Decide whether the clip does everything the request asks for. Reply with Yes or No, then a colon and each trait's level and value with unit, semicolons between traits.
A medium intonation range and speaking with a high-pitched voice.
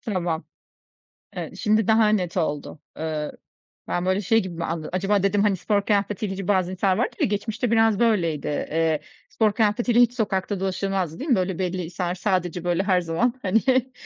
Yes: average, 3.5 semitones; high, 195 Hz